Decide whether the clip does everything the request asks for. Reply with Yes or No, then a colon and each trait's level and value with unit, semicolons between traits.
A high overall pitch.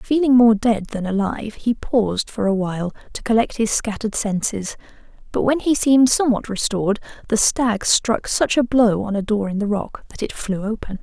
Yes: high, 220 Hz